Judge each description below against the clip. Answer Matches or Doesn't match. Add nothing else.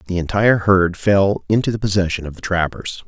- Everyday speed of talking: Matches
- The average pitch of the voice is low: Matches